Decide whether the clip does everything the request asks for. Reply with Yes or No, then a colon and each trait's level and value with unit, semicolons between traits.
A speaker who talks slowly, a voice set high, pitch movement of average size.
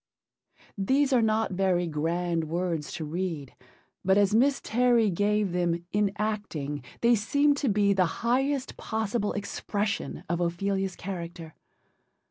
Yes: slow, 130 wpm; high, 195 Hz; average, 4.2 semitones